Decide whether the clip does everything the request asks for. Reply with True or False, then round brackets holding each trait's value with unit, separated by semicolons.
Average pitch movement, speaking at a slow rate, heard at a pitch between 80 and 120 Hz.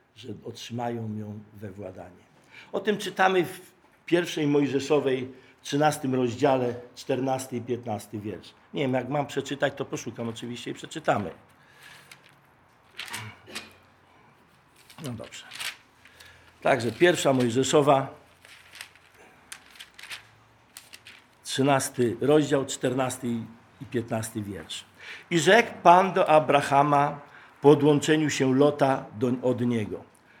False (3.7 semitones; 100 wpm; 135 Hz)